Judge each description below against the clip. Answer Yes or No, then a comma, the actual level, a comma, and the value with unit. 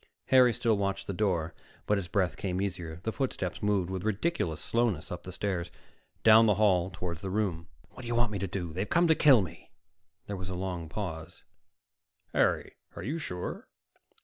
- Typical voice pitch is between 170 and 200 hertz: No, very low, 95 Hz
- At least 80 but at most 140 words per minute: No, average, 195 wpm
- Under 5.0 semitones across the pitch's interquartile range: Yes, average, 3.6 semitones